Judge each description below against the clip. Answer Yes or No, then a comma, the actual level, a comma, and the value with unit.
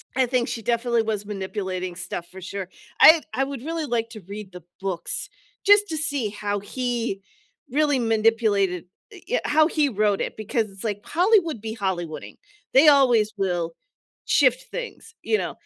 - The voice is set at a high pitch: Yes, high, 225 Hz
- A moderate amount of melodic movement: No, wide, 6.0 semitones